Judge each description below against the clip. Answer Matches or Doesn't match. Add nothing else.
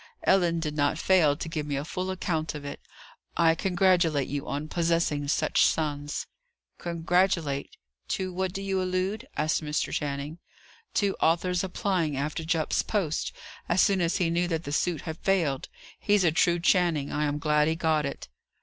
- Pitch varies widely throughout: Doesn't match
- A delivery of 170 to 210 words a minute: Matches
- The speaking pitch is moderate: Matches